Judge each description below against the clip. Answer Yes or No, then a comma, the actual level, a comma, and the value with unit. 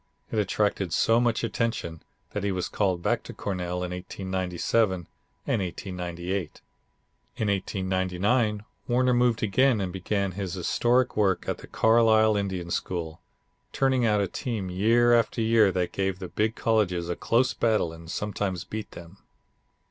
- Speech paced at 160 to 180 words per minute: No, average, 150 wpm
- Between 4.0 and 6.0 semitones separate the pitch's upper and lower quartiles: No, average, 3.6 semitones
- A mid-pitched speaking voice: No, low, 100 Hz